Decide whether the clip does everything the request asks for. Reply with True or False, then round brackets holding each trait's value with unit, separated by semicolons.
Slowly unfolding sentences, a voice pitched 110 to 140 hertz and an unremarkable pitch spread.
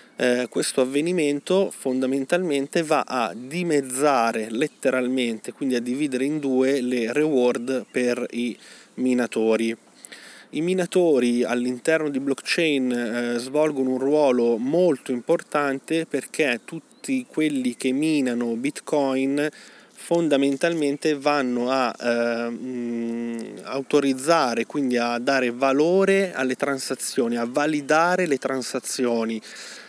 True (100 wpm; 135 Hz; 3.8 semitones)